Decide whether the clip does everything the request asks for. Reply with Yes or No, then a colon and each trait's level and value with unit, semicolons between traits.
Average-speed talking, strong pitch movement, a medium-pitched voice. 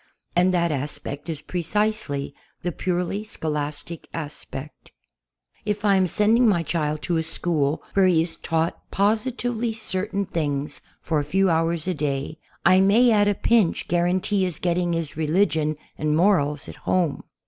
No: average, 160 wpm; average, 4.5 semitones; medium, 175 Hz